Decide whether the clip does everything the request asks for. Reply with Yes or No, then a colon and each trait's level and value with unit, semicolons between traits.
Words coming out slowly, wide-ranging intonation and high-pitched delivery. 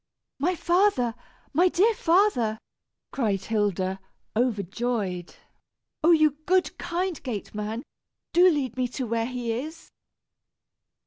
Yes: slow, 110 wpm; wide, 7.7 semitones; very high, 250 Hz